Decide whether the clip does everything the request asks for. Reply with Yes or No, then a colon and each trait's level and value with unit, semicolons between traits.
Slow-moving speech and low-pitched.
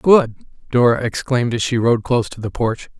No: average, 200 wpm; low, 120 Hz